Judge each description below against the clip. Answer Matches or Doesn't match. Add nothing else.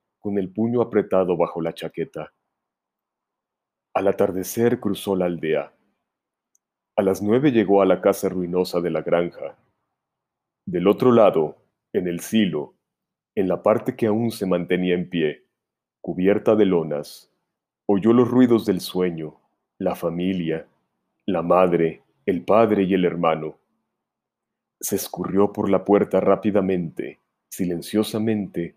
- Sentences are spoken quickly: Doesn't match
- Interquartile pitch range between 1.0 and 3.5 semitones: Matches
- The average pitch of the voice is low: Matches